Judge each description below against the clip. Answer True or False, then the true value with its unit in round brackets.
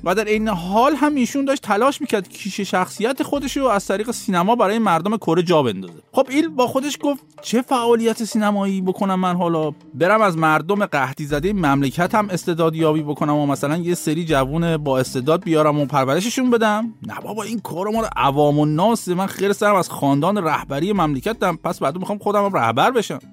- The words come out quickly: True (190 wpm)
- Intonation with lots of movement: True (6.0 semitones)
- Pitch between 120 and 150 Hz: False (190 Hz)